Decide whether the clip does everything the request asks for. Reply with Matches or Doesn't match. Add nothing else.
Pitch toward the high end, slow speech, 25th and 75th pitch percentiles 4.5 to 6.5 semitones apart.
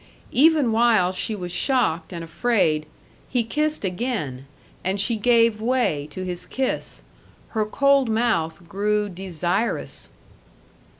Matches